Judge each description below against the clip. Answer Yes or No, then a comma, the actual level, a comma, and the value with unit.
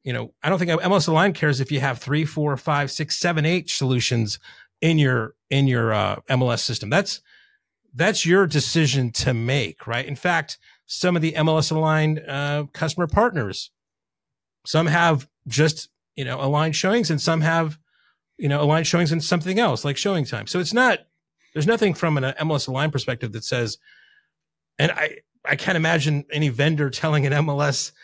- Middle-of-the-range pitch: Yes, medium, 150 Hz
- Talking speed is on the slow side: No, average, 180 wpm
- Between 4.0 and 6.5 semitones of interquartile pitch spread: No, average, 3.4 semitones